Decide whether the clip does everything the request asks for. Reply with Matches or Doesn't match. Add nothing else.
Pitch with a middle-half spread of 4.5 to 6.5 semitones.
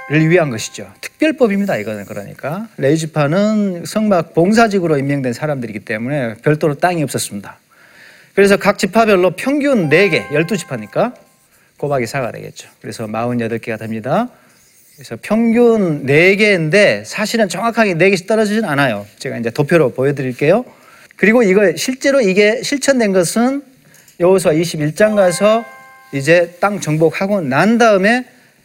Doesn't match